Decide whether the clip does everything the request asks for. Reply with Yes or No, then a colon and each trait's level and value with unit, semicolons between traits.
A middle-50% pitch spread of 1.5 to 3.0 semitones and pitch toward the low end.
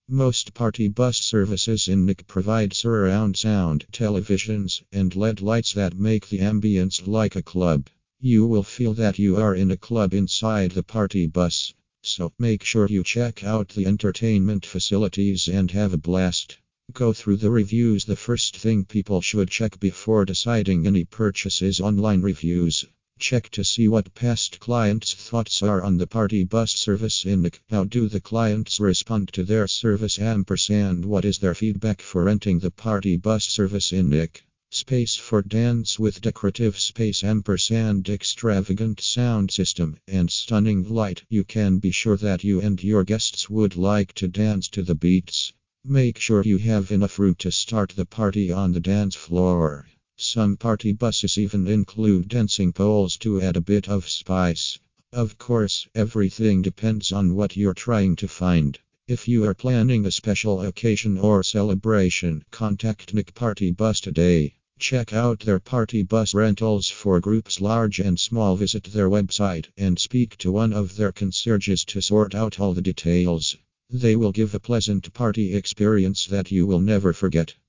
Yes: average, 2.7 semitones; low, 100 Hz